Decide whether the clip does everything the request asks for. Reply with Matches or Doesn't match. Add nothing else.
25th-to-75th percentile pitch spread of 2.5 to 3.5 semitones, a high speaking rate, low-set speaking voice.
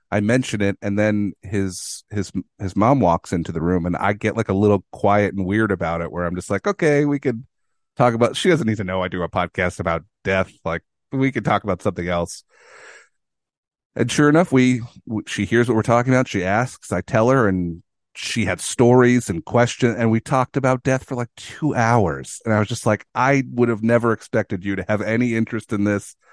Doesn't match